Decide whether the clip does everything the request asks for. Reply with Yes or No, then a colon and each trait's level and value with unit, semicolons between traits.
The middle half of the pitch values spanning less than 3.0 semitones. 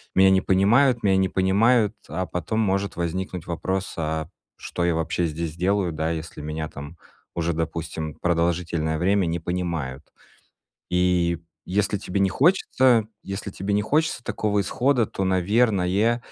No: average, 3.5 semitones